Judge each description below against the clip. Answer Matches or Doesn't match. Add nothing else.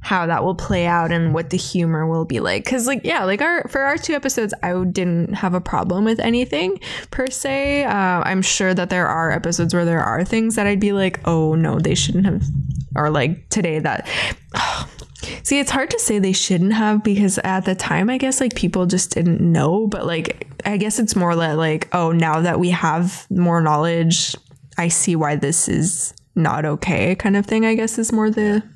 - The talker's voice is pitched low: Doesn't match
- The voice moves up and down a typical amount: Matches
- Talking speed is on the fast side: Matches